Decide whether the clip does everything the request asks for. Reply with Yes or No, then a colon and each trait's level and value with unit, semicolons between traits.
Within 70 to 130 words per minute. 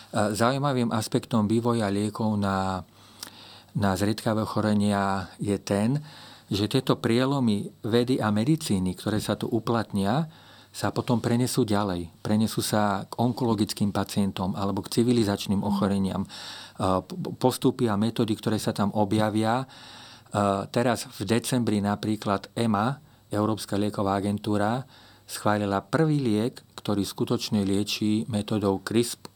Yes: average, 115 wpm